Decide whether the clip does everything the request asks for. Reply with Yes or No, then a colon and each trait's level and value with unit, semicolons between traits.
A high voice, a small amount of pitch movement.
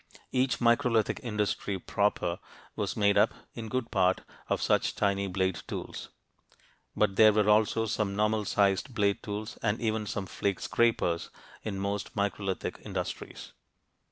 No: low, 105 Hz; narrow, 1.9 semitones